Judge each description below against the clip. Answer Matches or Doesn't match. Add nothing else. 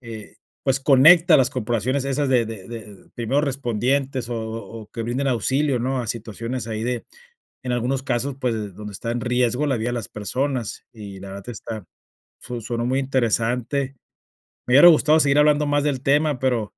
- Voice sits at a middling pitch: Doesn't match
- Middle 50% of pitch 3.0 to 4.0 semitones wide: Matches